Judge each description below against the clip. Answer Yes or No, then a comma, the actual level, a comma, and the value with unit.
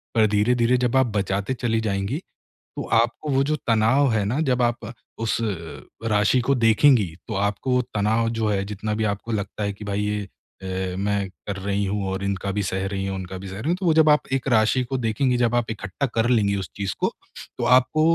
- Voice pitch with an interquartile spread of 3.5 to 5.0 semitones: Yes, average, 3.8 semitones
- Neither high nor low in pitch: No, low, 110 Hz